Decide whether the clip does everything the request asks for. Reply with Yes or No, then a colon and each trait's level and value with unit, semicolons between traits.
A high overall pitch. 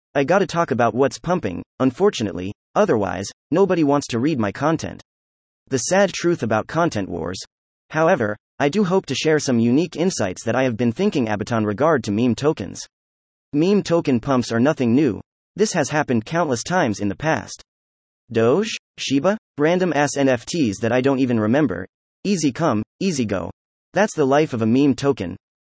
No: low, 135 Hz